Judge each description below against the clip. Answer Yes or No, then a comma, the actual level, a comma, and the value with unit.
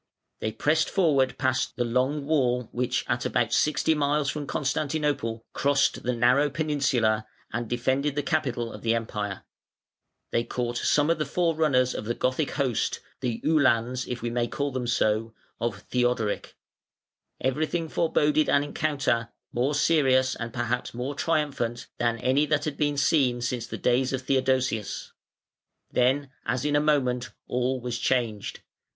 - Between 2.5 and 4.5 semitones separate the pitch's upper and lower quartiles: Yes, average, 3.5 semitones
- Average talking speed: Yes, average, 155 wpm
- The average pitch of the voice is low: Yes, low, 130 Hz